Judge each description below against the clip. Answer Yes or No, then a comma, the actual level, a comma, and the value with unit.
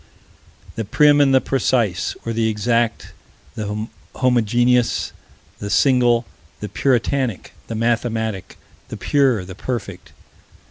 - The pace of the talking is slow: Yes, slow, 110 wpm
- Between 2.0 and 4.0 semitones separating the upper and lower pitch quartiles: Yes, average, 2.9 semitones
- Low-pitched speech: Yes, low, 115 Hz